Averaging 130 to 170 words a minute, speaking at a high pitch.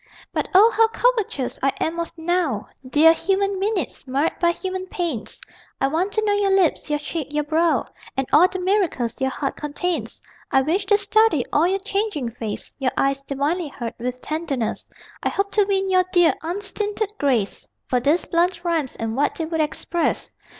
No: average, 185 wpm; very high, 335 Hz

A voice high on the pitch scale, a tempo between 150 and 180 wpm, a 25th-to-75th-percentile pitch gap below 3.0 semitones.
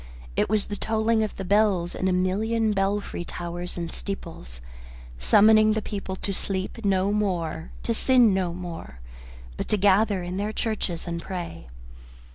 No: high, 195 Hz; average, 160 wpm; average, 3.4 semitones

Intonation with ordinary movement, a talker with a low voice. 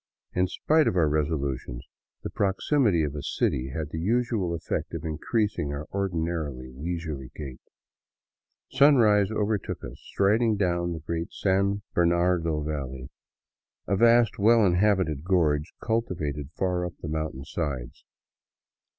Yes: average, 5.0 semitones; very low, 85 Hz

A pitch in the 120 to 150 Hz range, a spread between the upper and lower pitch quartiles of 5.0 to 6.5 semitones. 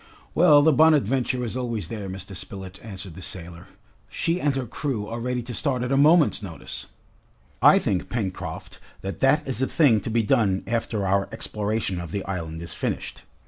No: low, 110 Hz; wide, 5.6 semitones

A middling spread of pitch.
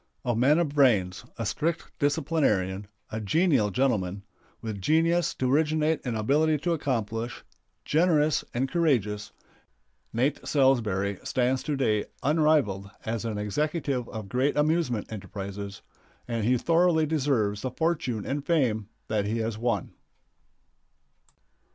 No: wide, 6.2 semitones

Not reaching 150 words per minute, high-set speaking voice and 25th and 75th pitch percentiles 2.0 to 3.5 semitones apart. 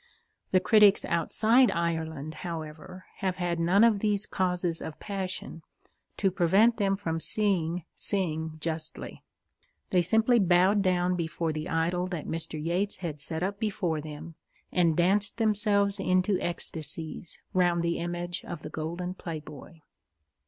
No: average, 140 wpm; medium, 175 Hz; average, 3.2 semitones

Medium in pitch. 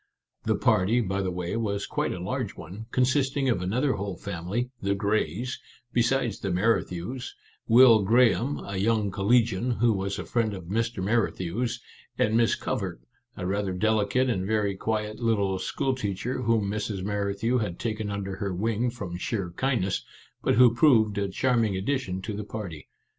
No: low, 105 Hz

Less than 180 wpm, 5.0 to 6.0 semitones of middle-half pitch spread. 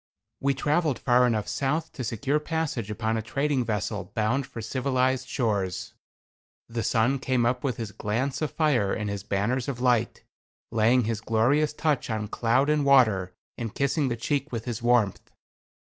No: average, 170 wpm; average, 3.8 semitones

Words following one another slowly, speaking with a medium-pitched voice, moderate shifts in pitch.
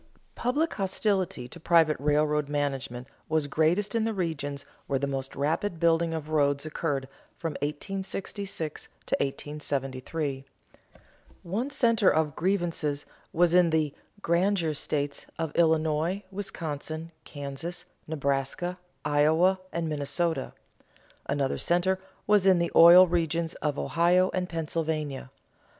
Yes: slow, 120 wpm; medium, 160 Hz; average, 3.5 semitones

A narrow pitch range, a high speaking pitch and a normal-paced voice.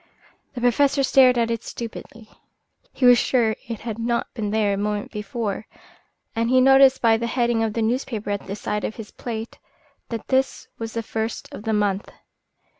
Yes: narrow, 2.3 semitones; high, 230 Hz; average, 190 wpm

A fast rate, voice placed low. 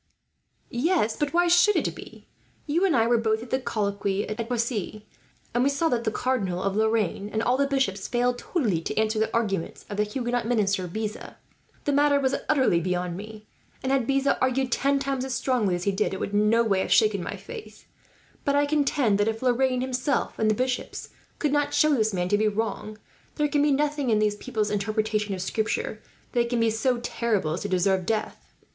No: fast, 215 wpm; high, 230 Hz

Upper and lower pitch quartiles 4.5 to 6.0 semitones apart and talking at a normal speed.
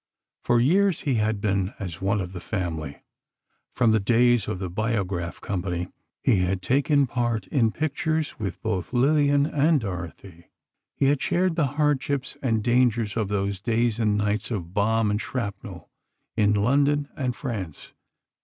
Yes: wide, 5.5 semitones; average, 155 wpm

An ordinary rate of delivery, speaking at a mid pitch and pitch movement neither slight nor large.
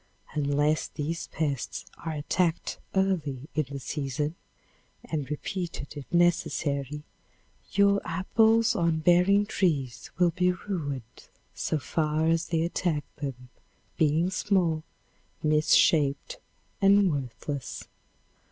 No: slow, 105 wpm; medium, 160 Hz; average, 3.7 semitones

